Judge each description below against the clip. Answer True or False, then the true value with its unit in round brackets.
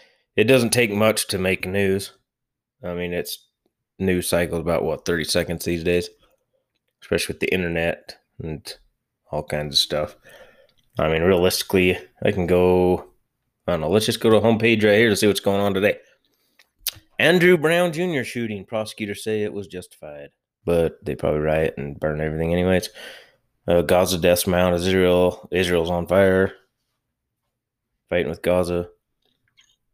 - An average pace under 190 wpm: True (155 wpm)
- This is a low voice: True (90 Hz)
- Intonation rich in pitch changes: False (3.7 semitones)